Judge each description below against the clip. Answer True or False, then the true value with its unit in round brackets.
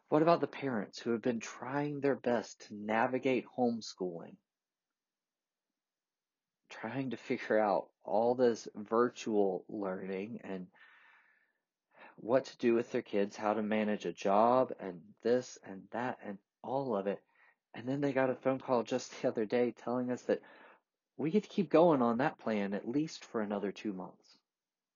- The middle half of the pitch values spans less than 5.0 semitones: True (3.5 semitones)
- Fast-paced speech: False (165 wpm)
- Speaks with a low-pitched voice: True (120 Hz)